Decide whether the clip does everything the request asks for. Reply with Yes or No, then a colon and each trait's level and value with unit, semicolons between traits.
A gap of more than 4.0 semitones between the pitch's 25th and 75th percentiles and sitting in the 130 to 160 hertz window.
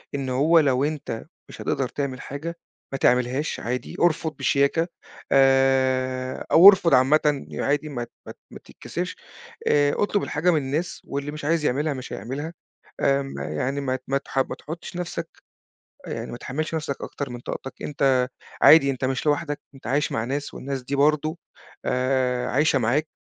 No: average, 2.8 semitones; medium, 140 Hz